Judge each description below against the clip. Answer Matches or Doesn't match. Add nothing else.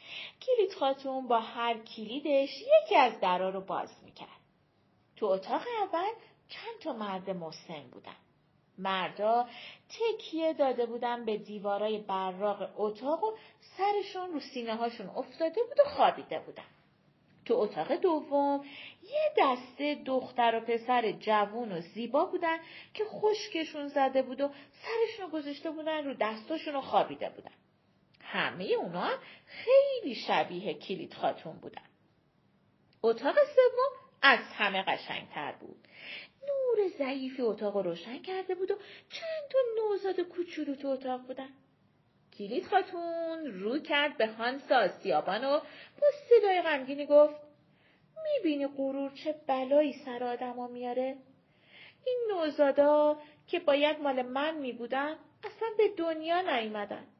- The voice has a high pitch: Matches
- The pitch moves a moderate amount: Doesn't match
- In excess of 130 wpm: Doesn't match